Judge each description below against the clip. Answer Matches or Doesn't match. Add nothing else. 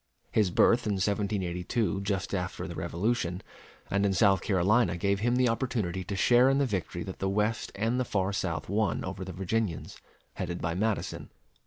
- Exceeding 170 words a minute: Matches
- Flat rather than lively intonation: Doesn't match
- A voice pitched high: Doesn't match